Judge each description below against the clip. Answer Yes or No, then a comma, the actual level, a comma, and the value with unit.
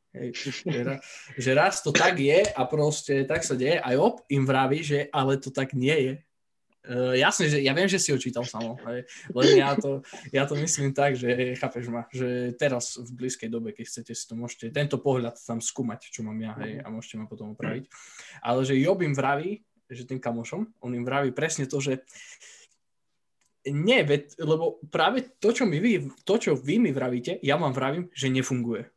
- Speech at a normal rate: No, fast, 195 wpm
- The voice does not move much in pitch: No, average, 3.2 semitones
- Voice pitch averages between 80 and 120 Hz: No, low, 135 Hz